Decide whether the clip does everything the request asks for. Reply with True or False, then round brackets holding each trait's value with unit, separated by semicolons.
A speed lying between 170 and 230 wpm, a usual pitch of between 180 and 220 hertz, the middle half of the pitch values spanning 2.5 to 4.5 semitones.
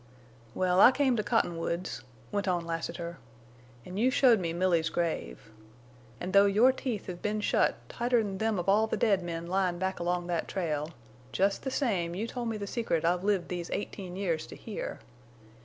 True (185 wpm; 190 Hz; 3.7 semitones)